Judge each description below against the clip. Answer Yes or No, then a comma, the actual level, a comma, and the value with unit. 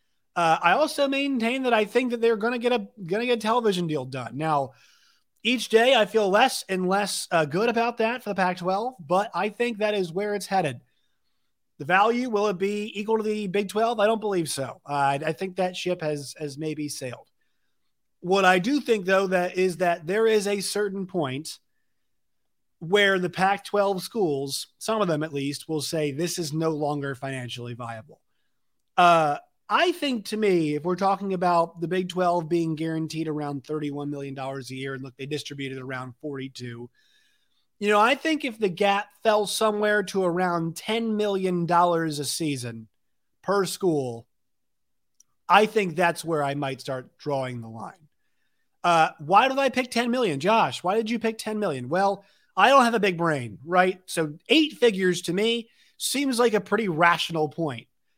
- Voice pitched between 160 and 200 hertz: Yes, medium, 185 Hz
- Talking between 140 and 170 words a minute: No, average, 190 wpm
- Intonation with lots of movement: Yes, wide, 5.9 semitones